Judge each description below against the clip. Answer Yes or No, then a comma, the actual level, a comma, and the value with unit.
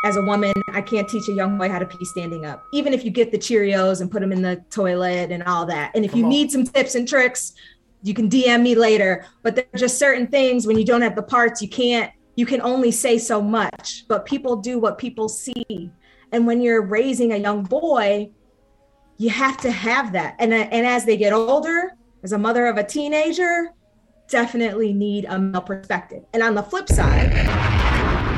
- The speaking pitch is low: No, high, 225 Hz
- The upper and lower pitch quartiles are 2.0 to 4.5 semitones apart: Yes, average, 3.4 semitones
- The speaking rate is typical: No, fast, 215 wpm